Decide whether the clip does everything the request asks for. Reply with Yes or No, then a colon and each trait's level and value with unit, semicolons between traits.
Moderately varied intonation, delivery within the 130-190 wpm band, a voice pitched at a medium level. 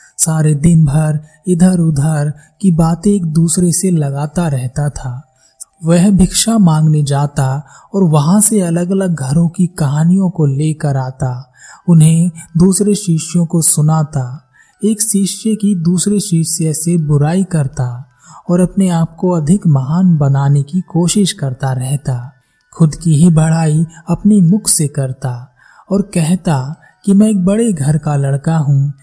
Yes: average, 3.9 semitones; average, 145 wpm; medium, 165 Hz